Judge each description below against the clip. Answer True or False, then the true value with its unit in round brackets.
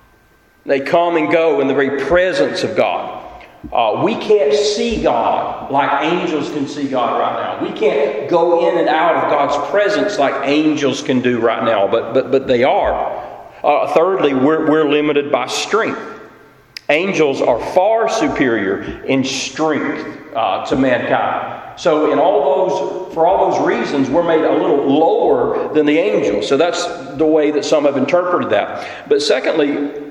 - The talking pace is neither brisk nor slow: True (170 wpm)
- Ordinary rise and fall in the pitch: True (3.7 semitones)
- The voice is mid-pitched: True (150 Hz)